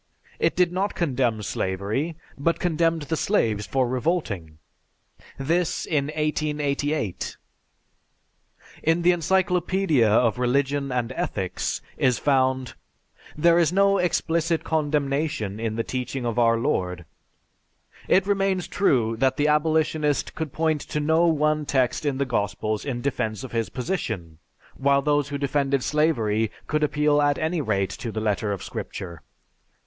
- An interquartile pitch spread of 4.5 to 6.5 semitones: Yes, wide, 5.5 semitones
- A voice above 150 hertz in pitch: No, medium, 140 Hz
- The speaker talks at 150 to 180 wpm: No, average, 140 wpm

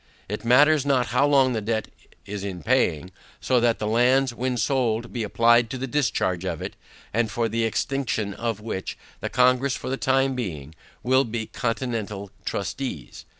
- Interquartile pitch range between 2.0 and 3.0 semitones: No, average, 3.5 semitones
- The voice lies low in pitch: Yes, low, 120 Hz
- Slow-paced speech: No, average, 180 wpm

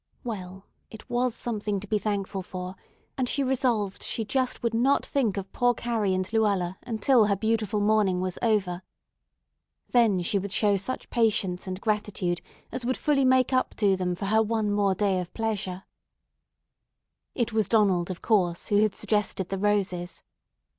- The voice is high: Yes, high, 210 Hz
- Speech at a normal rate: Yes, average, 170 wpm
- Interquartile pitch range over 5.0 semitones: No, average, 3.2 semitones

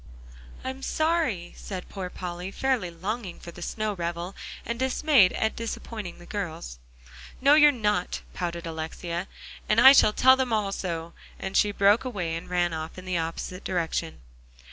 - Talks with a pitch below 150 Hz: No, high, 190 Hz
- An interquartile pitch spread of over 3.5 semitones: Yes, average, 5.1 semitones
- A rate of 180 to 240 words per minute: No, average, 165 wpm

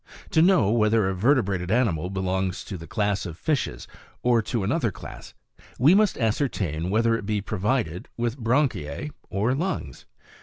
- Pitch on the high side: No, low, 110 Hz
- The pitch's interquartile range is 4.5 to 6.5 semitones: Yes, average, 4.9 semitones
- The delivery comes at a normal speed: Yes, average, 155 wpm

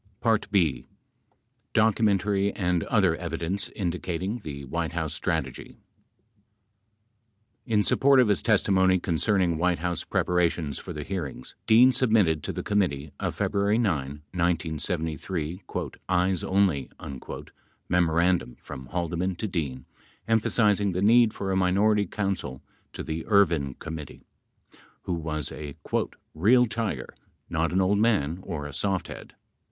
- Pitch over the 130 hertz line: No, very low, 90 Hz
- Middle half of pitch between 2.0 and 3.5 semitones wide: No, average, 4.1 semitones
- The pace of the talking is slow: Yes, slow, 125 wpm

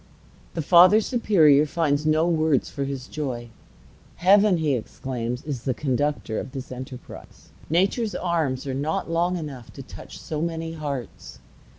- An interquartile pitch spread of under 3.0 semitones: No, average, 4.2 semitones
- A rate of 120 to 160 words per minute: Yes, average, 150 wpm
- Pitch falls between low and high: Yes, medium, 150 Hz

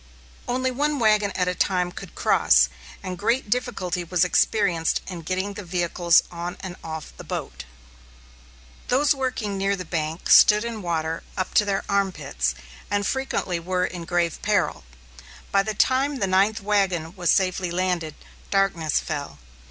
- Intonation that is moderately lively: Yes, average, 3.3 semitones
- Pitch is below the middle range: No, medium, 185 Hz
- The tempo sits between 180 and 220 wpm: No, average, 160 wpm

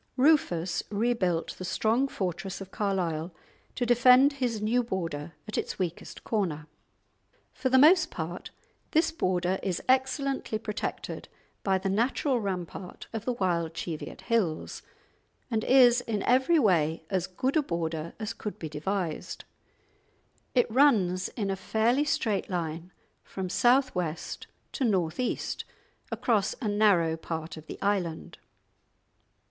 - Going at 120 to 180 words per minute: Yes, slow, 135 wpm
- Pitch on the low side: No, high, 200 Hz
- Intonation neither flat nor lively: No, wide, 6.0 semitones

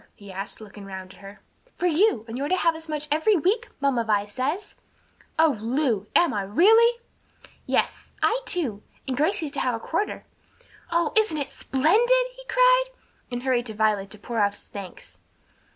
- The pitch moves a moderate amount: No, wide, 9.0 semitones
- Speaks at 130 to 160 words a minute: No, average, 185 wpm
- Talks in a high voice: Yes, very high, 280 Hz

